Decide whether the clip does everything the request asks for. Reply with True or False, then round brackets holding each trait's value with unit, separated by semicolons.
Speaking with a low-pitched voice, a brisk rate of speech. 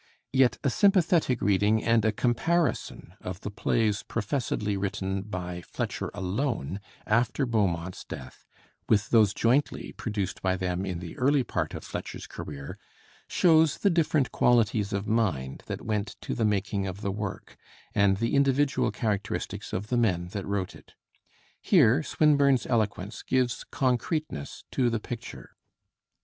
False (110 Hz; 145 wpm)